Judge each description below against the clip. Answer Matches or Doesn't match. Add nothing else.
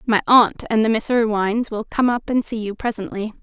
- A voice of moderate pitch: Doesn't match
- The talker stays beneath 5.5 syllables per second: Doesn't match